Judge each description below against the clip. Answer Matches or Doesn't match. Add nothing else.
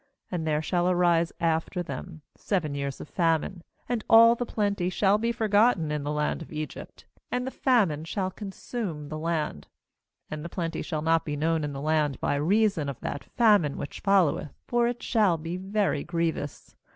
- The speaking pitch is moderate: Matches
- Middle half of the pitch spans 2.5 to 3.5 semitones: Doesn't match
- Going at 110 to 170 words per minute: Doesn't match